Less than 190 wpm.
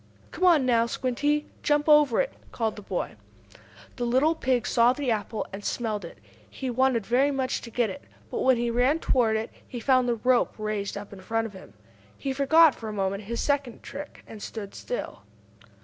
No: average, 200 wpm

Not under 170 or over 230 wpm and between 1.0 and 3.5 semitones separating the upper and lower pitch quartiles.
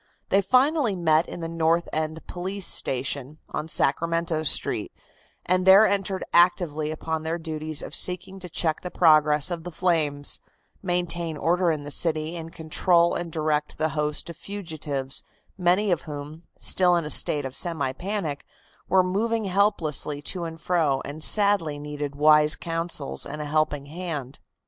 No: average, 160 wpm; average, 2.9 semitones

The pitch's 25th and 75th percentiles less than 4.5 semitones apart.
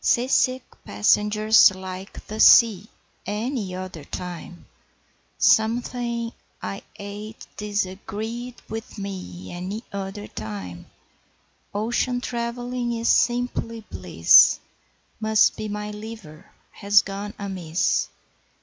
Yes: average, 3.7 semitones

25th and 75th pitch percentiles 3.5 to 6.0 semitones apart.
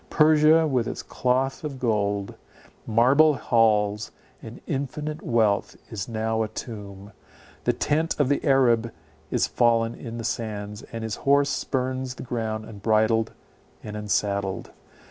Yes: average, 3.8 semitones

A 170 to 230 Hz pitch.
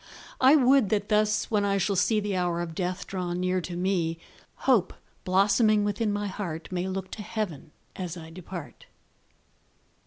Yes: high, 190 Hz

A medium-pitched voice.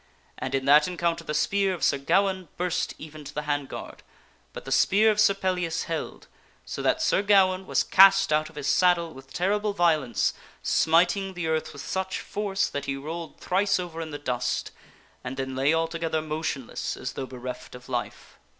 Yes: medium, 165 Hz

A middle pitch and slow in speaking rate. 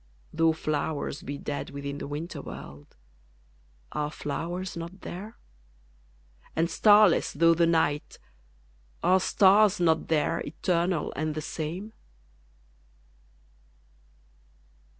Yes: medium, 165 Hz; slow, 100 wpm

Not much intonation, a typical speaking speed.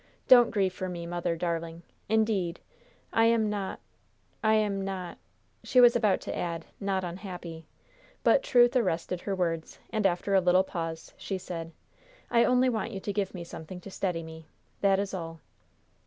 No: average, 3.9 semitones; average, 175 wpm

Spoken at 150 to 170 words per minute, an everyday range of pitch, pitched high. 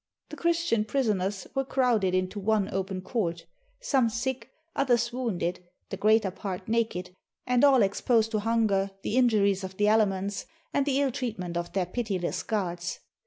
Yes: average, 160 wpm; average, 4.3 semitones; high, 215 Hz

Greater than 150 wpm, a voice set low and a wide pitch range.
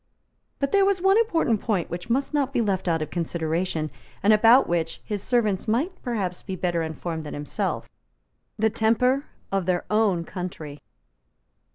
No: average, 165 wpm; high, 200 Hz; wide, 6.2 semitones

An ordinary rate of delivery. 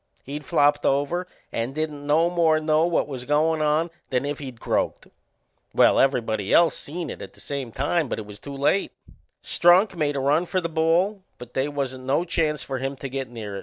No: fast, 210 wpm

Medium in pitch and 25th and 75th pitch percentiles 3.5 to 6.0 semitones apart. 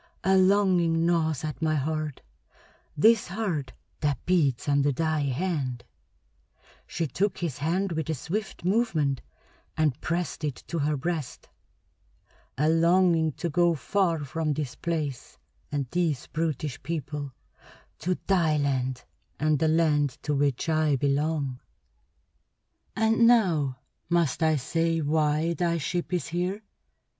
No: medium, 160 Hz; average, 3.1 semitones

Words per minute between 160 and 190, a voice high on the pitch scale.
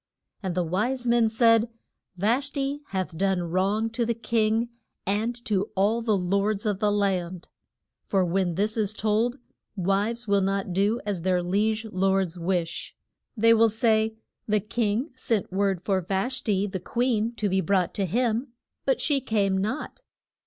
Yes: average, 165 wpm; high, 205 Hz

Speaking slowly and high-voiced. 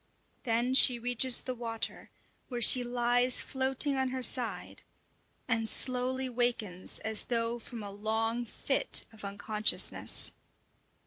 Yes: slow, 125 wpm; high, 240 Hz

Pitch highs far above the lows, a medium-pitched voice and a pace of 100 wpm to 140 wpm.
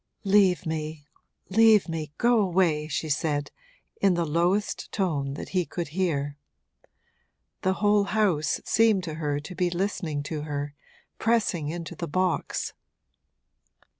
No: average, 4.3 semitones; medium, 170 Hz; slow, 135 wpm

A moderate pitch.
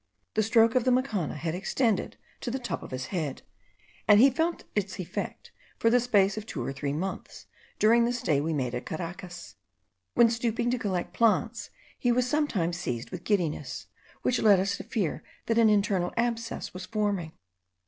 No: high, 205 Hz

